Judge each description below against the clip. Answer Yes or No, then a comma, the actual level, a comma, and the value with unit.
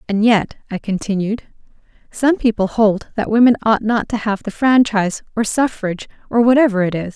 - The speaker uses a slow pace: No, average, 175 wpm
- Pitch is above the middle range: Yes, high, 215 Hz